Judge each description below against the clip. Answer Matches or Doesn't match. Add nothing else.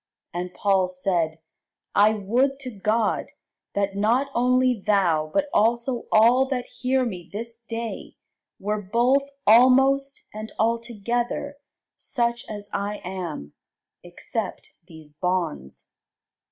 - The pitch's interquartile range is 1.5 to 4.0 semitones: Doesn't match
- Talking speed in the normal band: Doesn't match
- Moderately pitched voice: Doesn't match